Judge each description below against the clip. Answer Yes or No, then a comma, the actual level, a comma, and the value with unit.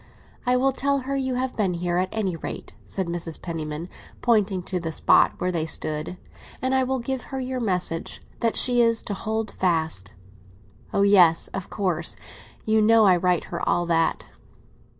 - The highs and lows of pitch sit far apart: Yes, wide, 5.9 semitones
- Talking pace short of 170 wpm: No, average, 175 wpm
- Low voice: No, high, 195 Hz